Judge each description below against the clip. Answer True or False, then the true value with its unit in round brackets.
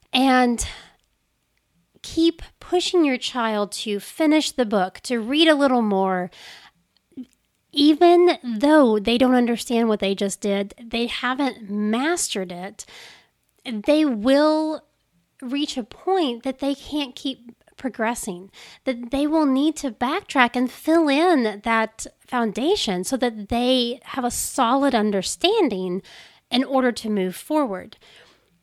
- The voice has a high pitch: True (250 Hz)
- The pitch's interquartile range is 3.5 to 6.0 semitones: True (5.0 semitones)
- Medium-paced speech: False (125 wpm)